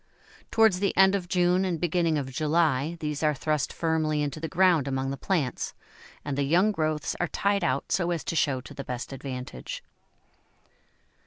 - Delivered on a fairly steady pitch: No, average, 4.2 semitones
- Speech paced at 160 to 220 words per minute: Yes, average, 180 wpm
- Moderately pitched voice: Yes, medium, 155 Hz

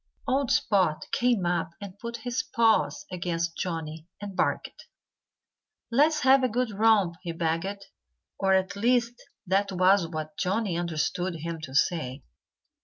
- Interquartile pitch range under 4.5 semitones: No, average, 5.1 semitones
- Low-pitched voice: No, high, 190 Hz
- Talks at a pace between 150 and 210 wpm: No, average, 140 wpm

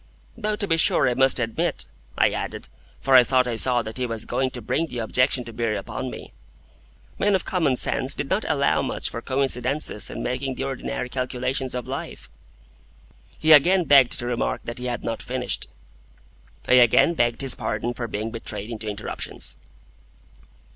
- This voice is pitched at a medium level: No, low, 125 Hz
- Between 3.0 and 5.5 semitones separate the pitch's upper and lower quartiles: No, narrow, 2.4 semitones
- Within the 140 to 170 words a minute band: No, average, 180 wpm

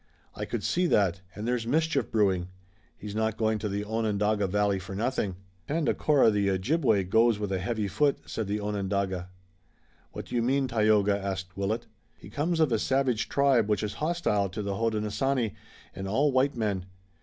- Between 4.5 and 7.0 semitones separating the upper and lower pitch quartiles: No, average, 3.8 semitones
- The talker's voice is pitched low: Yes, low, 105 Hz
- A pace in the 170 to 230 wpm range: Yes, average, 180 wpm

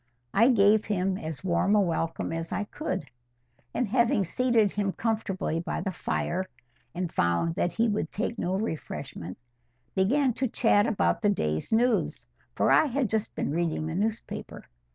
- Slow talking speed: No, average, 165 wpm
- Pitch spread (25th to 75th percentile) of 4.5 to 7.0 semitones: Yes, average, 4.8 semitones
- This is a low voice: No, high, 200 Hz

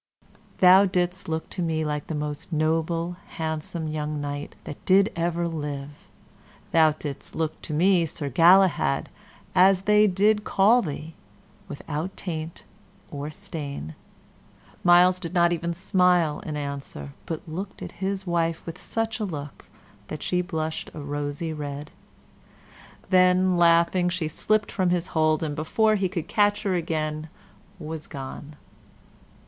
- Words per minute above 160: No, average, 140 wpm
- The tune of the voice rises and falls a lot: No, average, 3.2 semitones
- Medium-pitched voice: Yes, medium, 165 Hz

